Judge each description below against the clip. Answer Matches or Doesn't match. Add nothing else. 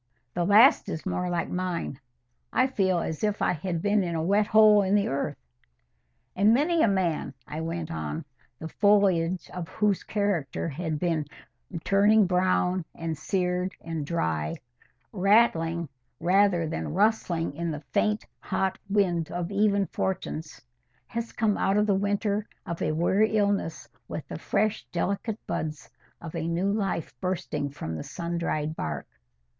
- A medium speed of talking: Matches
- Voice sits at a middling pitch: Matches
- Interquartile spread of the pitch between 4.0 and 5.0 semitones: Doesn't match